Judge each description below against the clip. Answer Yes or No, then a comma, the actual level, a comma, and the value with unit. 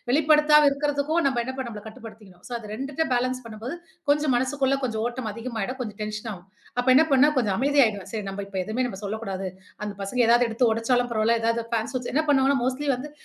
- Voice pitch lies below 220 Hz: No, high, 245 Hz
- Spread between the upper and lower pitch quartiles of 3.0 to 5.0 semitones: Yes, average, 3.8 semitones